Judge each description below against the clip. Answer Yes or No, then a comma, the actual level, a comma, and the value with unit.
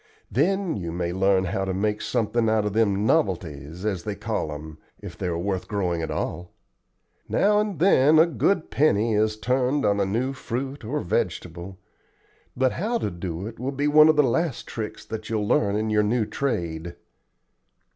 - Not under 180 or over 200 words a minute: Yes, average, 185 wpm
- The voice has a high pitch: No, low, 110 Hz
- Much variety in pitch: Yes, wide, 6.3 semitones